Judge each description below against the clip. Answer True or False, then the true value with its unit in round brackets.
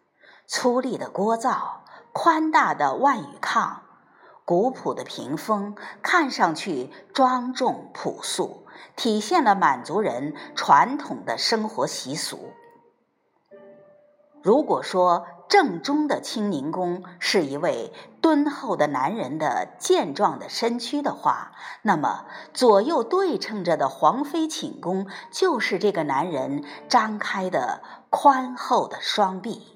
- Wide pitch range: True (7.6 semitones)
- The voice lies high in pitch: True (255 Hz)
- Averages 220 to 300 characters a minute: False (175 characters per minute)